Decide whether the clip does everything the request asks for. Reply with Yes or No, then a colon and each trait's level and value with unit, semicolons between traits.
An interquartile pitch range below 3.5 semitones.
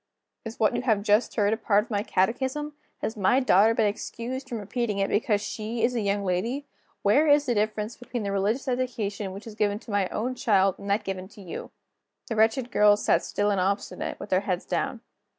Yes: average, 3.0 semitones